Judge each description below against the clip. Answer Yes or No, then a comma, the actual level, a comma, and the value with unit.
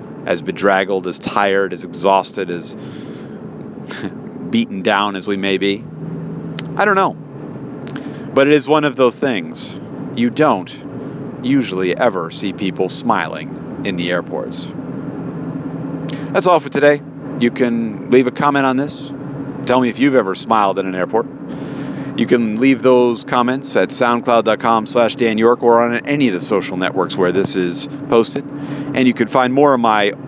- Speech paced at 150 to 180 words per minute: Yes, average, 160 wpm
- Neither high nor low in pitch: No, low, 120 Hz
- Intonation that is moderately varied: No, wide, 5.7 semitones